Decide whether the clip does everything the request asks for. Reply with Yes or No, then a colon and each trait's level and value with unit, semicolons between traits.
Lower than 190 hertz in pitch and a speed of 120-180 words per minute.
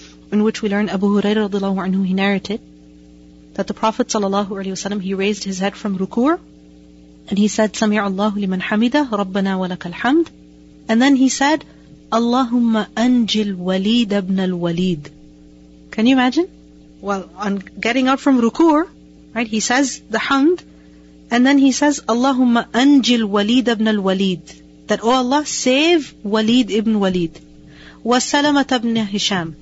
No: high, 210 Hz; average, 150 wpm